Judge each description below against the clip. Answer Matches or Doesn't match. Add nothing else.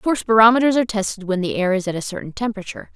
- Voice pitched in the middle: Doesn't match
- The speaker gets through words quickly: Matches